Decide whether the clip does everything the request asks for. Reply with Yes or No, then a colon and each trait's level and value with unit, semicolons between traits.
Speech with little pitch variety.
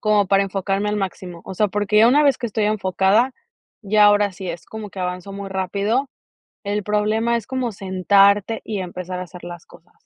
Yes: narrow, 2.1 semitones